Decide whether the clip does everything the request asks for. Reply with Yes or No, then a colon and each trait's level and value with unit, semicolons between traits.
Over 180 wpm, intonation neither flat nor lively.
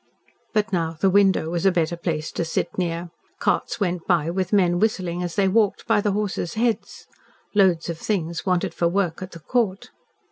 Yes: average, 190 wpm; average, 3.0 semitones